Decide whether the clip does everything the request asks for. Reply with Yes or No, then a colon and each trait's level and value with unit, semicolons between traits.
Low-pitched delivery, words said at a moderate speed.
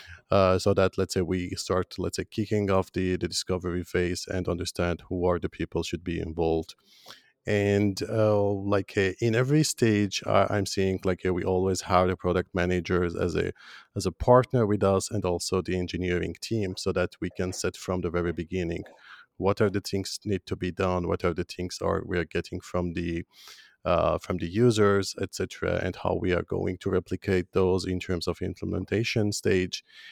Yes: very low, 95 Hz; average, 195 wpm